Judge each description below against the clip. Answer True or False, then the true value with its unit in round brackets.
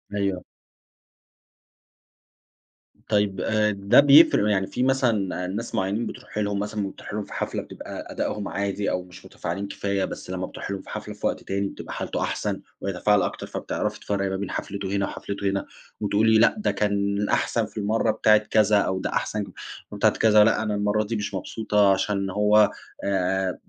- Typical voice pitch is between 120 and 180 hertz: False (100 Hz)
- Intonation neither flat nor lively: False (1.5 semitones)